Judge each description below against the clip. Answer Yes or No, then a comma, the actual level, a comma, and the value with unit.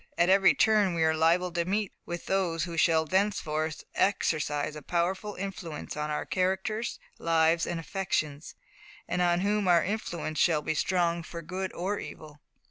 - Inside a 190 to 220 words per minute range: No, average, 165 wpm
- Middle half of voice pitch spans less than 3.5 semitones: Yes, average, 3.1 semitones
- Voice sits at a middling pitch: Yes, medium, 175 Hz